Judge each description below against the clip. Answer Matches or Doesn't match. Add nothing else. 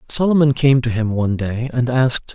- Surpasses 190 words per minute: Matches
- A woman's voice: Doesn't match